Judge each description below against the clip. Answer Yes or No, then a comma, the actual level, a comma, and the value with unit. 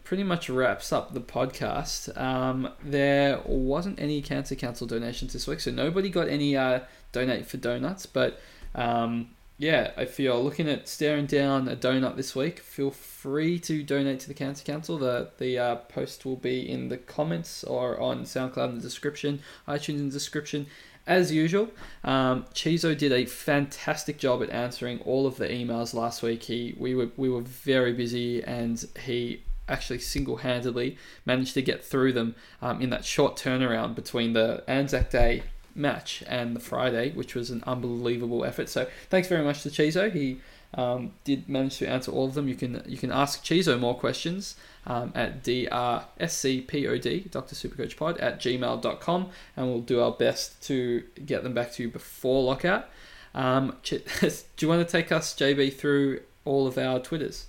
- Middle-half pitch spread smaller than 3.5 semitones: Yes, average, 2.9 semitones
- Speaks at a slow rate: No, average, 175 wpm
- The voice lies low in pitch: Yes, low, 130 Hz